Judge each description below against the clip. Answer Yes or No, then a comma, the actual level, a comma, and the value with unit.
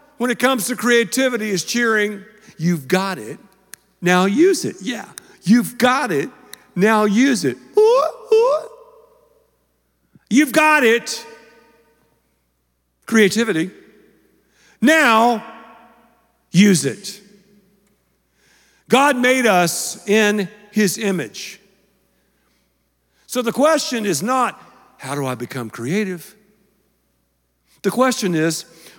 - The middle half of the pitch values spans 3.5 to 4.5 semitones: No, average, 5.3 semitones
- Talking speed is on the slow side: Yes, slow, 100 wpm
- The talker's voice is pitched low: No, high, 210 Hz